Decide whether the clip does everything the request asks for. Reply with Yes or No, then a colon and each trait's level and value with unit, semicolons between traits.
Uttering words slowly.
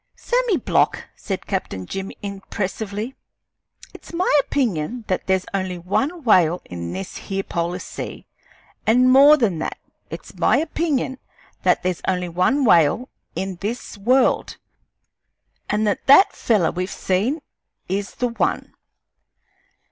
Yes: slow, 130 wpm